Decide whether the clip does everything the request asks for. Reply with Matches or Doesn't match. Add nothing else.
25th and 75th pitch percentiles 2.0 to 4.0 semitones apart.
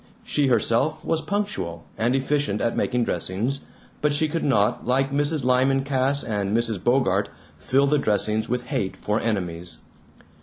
Doesn't match